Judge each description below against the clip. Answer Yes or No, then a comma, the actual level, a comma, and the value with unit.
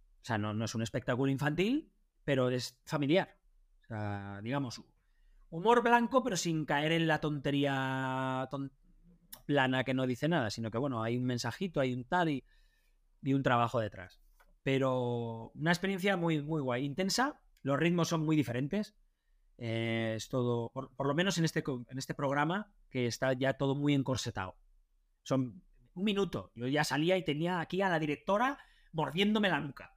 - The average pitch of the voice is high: No, medium, 140 Hz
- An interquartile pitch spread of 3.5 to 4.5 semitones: No, wide, 5.5 semitones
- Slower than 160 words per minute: No, average, 175 wpm